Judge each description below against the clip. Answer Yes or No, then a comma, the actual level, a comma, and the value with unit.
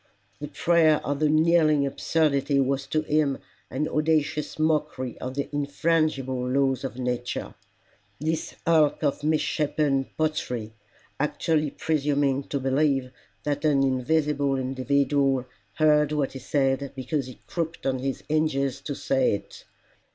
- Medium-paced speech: No, slow, 130 wpm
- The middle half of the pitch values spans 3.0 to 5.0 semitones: No, narrow, 2.4 semitones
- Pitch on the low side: No, medium, 145 Hz